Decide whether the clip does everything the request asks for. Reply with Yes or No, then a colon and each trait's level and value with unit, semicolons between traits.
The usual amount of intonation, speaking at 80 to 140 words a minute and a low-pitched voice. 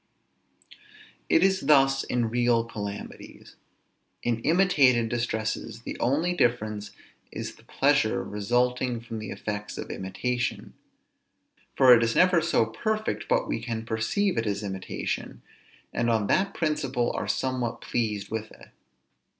Yes: average, 3.5 semitones; slow, 135 wpm; low, 120 Hz